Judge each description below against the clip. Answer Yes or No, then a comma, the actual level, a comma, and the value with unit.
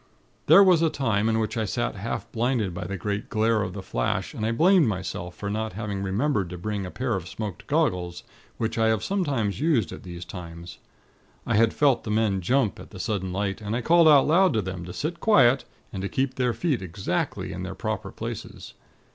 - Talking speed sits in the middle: No, fast, 220 wpm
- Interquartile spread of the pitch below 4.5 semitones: No, average, 5.3 semitones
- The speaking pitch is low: Yes, low, 110 Hz